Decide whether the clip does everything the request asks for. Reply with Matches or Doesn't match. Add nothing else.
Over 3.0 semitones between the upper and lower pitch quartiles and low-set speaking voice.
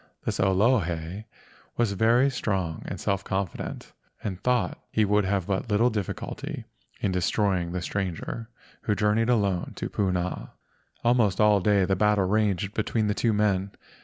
Doesn't match